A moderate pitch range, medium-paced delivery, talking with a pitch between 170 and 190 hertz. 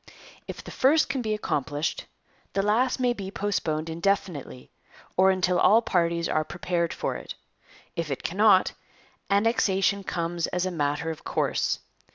Yes: average, 3.7 semitones; average, 150 wpm; medium, 185 Hz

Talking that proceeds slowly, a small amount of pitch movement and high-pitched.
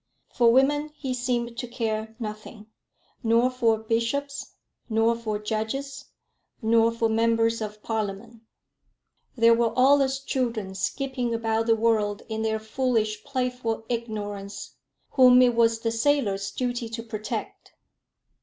Yes: slow, 130 wpm; narrow, 2.3 semitones; high, 230 Hz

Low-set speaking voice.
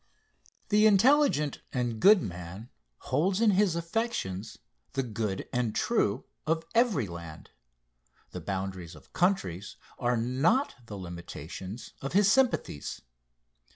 Yes: low, 125 Hz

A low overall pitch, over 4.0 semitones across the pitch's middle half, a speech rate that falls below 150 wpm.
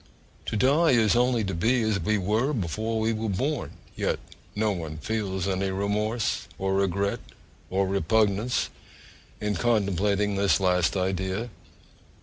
No: low, 105 Hz; average, 2.7 semitones; slow, 135 wpm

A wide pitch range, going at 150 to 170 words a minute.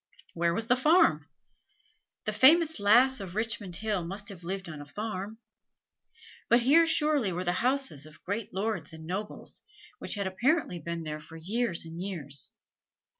Yes: wide, 5.9 semitones; average, 165 wpm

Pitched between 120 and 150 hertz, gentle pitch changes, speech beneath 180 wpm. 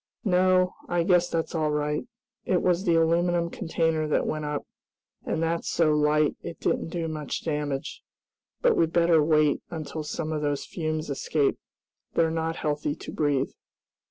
No: medium, 160 Hz; narrow, 2.1 semitones; average, 160 wpm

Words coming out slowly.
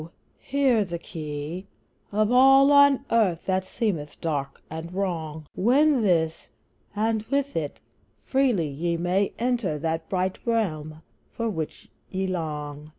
Yes: slow, 130 wpm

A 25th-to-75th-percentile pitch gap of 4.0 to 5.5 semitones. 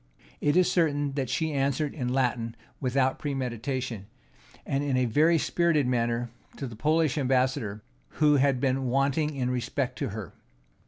No: average, 2.9 semitones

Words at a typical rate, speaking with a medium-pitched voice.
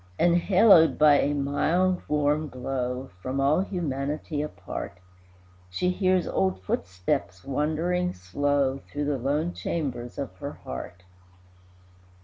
No: slow, 115 wpm; medium, 145 Hz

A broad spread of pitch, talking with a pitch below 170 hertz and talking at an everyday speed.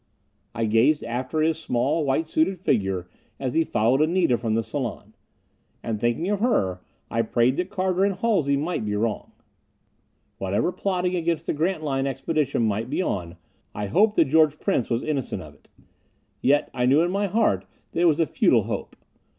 Yes: wide, 6.8 semitones; medium, 140 Hz; average, 180 wpm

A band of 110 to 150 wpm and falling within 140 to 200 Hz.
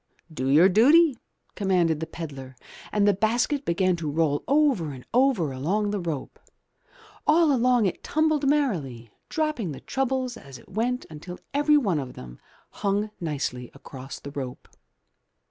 Yes: average, 145 wpm; high, 190 Hz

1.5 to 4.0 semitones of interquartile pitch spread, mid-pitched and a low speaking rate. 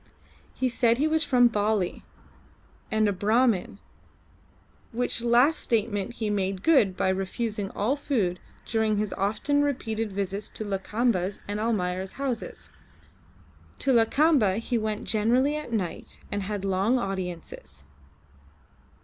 No: average, 3.7 semitones; high, 215 Hz; slow, 125 wpm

